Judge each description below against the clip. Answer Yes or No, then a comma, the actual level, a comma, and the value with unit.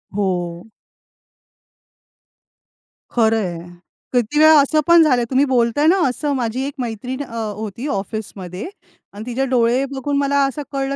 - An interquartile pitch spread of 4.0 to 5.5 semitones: Yes, average, 4.4 semitones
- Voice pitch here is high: Yes, very high, 250 Hz